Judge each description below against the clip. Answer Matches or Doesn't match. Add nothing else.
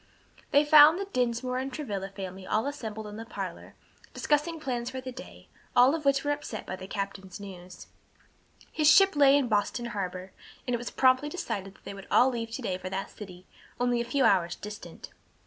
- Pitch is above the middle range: Matches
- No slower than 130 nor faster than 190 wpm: Doesn't match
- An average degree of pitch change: Doesn't match